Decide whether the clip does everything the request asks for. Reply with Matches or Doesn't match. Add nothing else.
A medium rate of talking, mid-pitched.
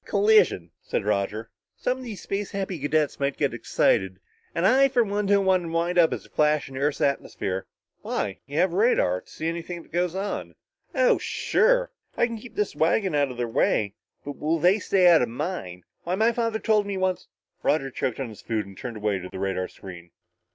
Doesn't match